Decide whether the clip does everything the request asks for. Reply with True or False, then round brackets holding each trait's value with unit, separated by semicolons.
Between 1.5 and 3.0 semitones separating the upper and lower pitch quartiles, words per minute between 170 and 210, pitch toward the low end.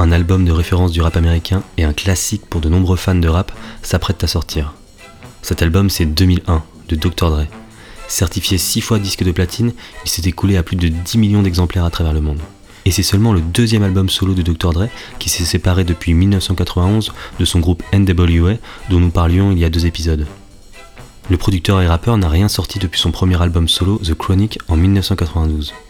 True (2.6 semitones; 205 wpm; 90 Hz)